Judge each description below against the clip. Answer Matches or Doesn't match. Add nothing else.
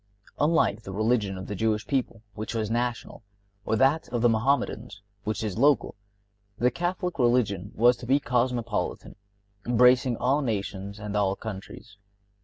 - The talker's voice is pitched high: Doesn't match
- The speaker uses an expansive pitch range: Doesn't match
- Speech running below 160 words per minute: Matches